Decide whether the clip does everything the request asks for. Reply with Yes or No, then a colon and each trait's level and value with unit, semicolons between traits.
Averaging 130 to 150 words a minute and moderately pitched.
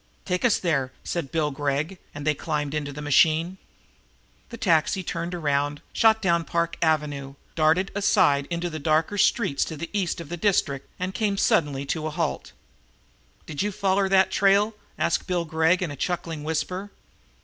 No: average, 170 wpm; medium, 165 Hz